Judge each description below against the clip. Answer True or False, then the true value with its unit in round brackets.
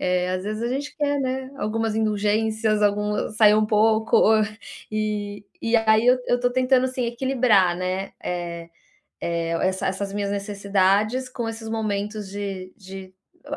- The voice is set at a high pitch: True (215 Hz)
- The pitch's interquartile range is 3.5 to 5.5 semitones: False (2.4 semitones)